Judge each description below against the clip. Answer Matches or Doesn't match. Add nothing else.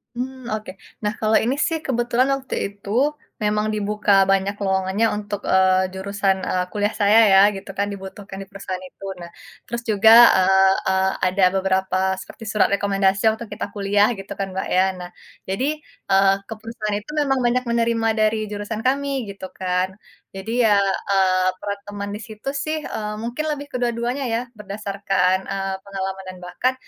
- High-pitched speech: Matches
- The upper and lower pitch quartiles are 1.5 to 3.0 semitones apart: Matches